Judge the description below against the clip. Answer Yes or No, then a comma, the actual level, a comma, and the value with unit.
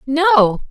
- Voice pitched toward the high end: Yes, very high, 285 Hz